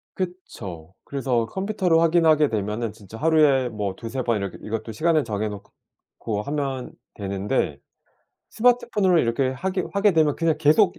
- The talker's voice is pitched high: No, low, 135 Hz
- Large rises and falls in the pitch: Yes, wide, 7.5 semitones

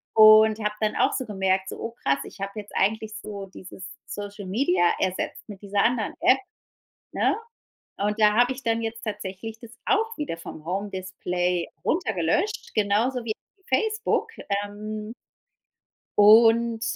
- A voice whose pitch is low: No, high, 215 Hz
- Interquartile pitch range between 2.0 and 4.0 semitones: Yes, average, 2.9 semitones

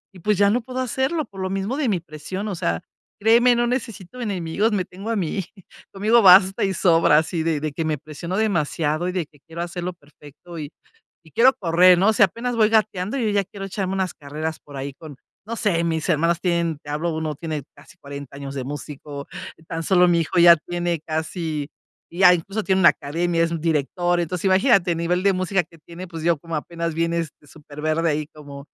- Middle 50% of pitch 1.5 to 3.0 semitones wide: No, average, 3.7 semitones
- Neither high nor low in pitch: Yes, medium, 170 Hz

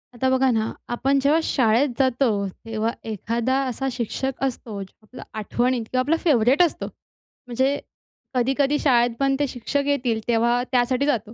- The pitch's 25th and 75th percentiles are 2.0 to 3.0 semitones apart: Yes, narrow, 2.6 semitones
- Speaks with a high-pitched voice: Yes, very high, 255 Hz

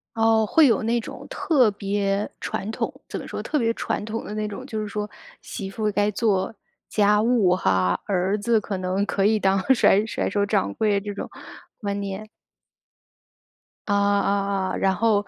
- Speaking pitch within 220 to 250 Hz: No, high, 205 Hz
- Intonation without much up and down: Yes, narrow, 1.9 semitones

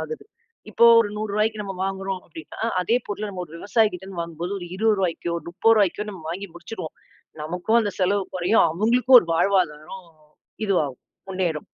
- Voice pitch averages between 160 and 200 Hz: Yes, high, 195 Hz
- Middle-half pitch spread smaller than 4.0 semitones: Yes, average, 3.5 semitones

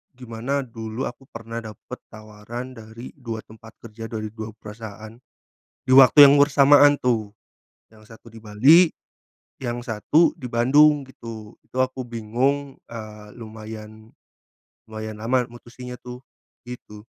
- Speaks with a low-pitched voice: Yes, low, 115 Hz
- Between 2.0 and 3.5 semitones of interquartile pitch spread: Yes, average, 2.9 semitones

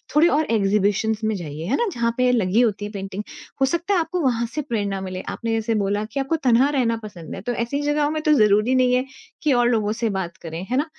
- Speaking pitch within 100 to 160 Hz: No, high, 230 Hz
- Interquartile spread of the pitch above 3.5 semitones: Yes, average, 4.9 semitones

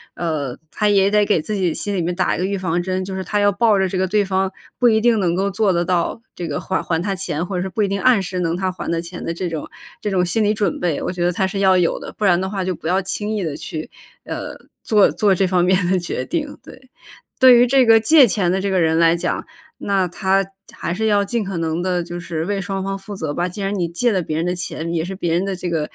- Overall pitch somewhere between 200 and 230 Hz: No, high, 190 Hz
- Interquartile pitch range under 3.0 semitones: Yes, narrow, 2.6 semitones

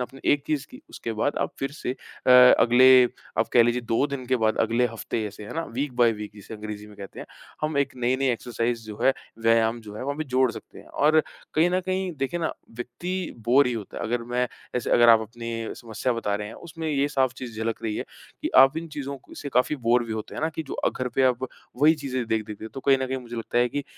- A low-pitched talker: Yes, low, 125 Hz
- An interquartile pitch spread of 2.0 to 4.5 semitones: Yes, average, 3.4 semitones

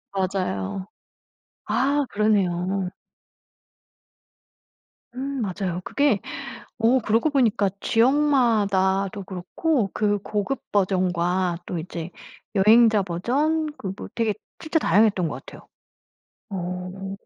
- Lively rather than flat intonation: No, average, 4.3 semitones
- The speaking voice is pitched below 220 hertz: Yes, high, 200 Hz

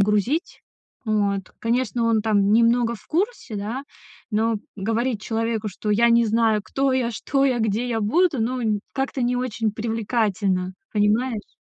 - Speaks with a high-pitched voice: Yes, high, 225 Hz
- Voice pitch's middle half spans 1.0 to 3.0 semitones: Yes, average, 2.7 semitones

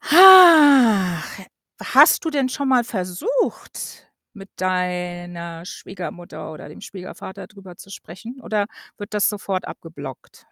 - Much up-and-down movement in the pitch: Yes, wide, 6.3 semitones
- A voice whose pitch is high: Yes, high, 195 Hz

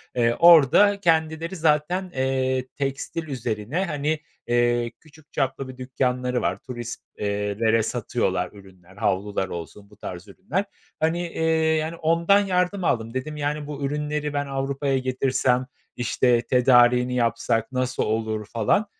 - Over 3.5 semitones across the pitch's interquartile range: Yes, average, 4.6 semitones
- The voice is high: No, low, 130 Hz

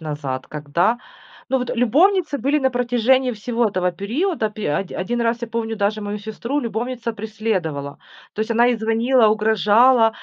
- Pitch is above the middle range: Yes, high, 225 Hz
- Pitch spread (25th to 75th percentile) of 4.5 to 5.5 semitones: No, average, 3.2 semitones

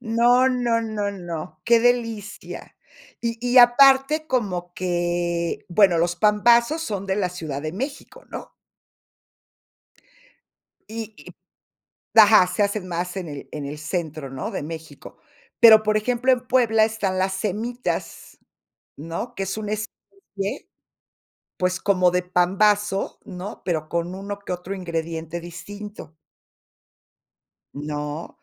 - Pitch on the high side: Yes, high, 195 Hz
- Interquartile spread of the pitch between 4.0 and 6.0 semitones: Yes, average, 4.5 semitones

